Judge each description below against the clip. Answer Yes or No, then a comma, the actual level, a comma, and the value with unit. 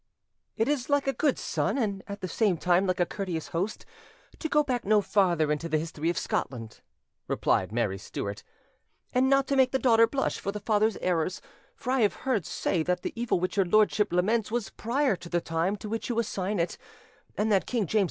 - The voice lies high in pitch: Yes, high, 205 Hz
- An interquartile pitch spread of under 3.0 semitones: No, average, 5.3 semitones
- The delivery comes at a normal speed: No, fast, 220 wpm